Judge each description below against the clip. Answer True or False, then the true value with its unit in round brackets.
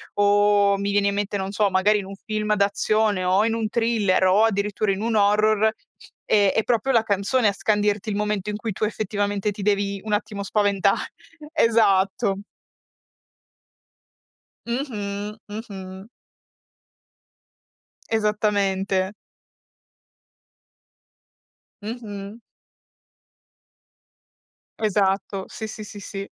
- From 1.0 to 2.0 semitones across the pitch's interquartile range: True (1.4 semitones)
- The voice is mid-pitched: False (205 Hz)